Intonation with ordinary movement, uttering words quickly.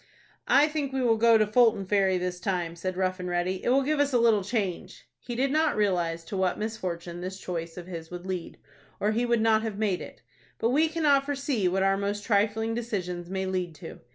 Yes: average, 4.6 semitones; fast, 225 wpm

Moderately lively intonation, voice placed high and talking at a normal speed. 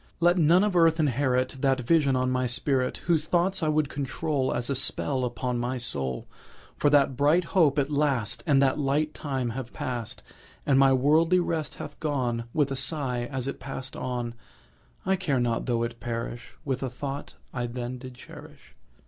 No: average, 3.3 semitones; low, 135 Hz; average, 185 wpm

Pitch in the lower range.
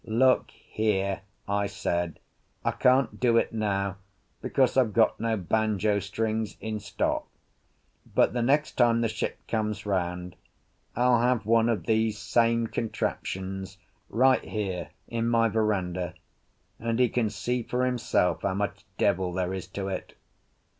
Yes: low, 110 Hz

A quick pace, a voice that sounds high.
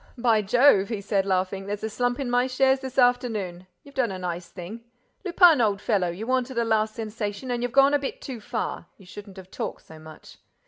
Yes: fast, 220 wpm; high, 225 Hz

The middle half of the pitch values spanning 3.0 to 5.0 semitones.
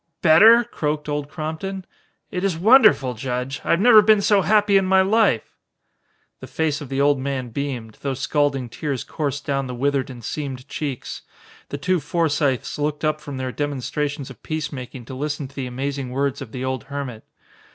Yes: average, 3.4 semitones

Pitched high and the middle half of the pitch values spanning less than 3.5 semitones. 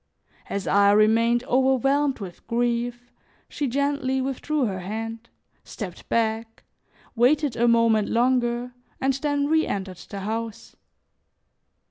Yes: high, 235 Hz; average, 3.1 semitones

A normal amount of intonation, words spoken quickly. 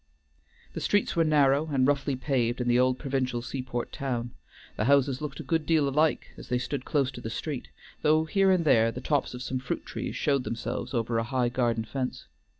Yes: average, 3.0 semitones; fast, 210 wpm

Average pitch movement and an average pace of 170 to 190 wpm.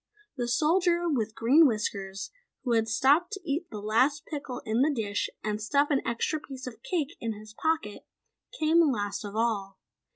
No: wide, 6.0 semitones; average, 175 wpm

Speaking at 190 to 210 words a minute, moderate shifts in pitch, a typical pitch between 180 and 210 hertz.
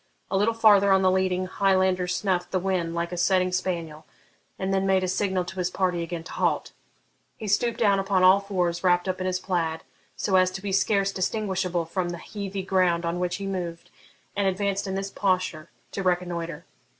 No: average, 200 wpm; narrow, 1.6 semitones; medium, 185 Hz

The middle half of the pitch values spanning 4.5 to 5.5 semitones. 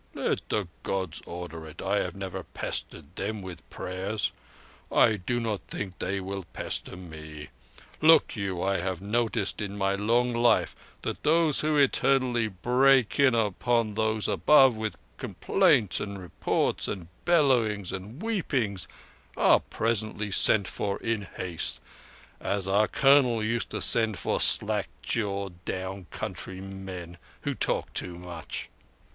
No: average, 4.0 semitones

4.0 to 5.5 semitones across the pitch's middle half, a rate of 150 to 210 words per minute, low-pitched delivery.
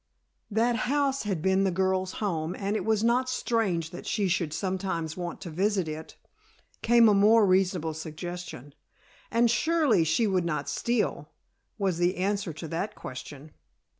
No: average, 4.4 semitones; average, 160 wpm; high, 190 Hz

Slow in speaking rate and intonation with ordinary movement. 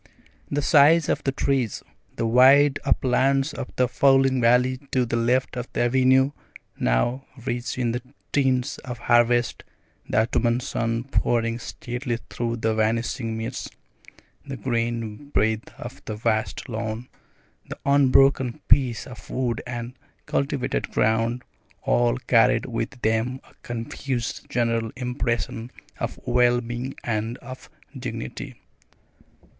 No: slow, 130 wpm; narrow, 2.1 semitones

